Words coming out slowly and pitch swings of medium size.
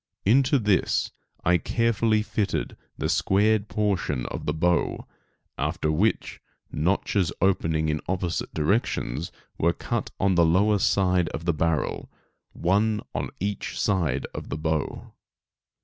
Yes: slow, 130 wpm; average, 4.4 semitones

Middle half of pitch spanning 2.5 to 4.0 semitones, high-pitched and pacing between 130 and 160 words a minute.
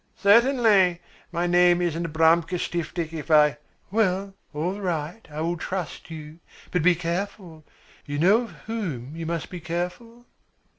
No: average, 3.1 semitones; medium, 175 Hz; average, 150 wpm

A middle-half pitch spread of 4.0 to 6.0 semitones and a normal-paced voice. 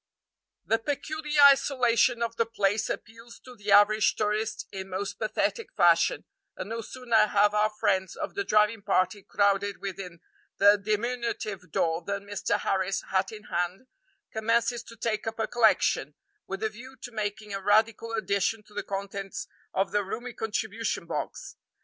No: narrow, 2.4 semitones; average, 160 wpm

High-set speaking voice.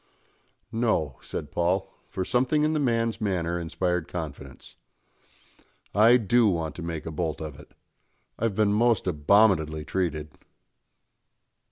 No: very low, 90 Hz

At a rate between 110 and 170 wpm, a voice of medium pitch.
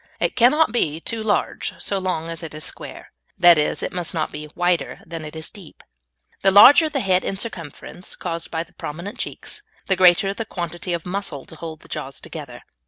No: fast, 205 wpm; medium, 175 Hz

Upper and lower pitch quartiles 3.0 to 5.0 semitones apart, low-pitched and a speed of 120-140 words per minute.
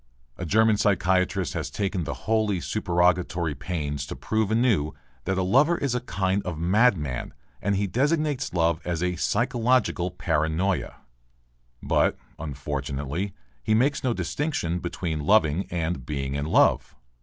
No: wide, 5.4 semitones; very low, 90 Hz; slow, 135 wpm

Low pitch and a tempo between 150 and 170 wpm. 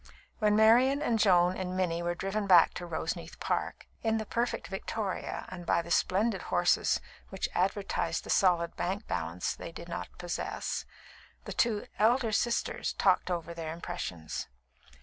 No: medium, 185 Hz; average, 155 wpm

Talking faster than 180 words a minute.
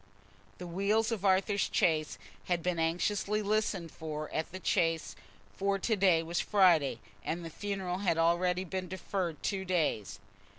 No: average, 155 wpm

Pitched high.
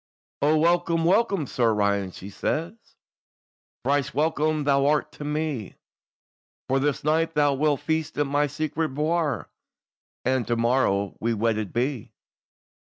No: medium, 145 Hz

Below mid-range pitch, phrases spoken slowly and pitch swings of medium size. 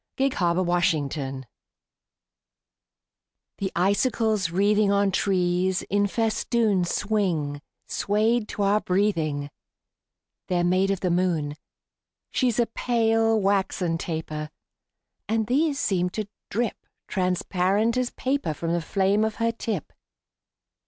No: high, 195 Hz; slow, 110 wpm; average, 3.9 semitones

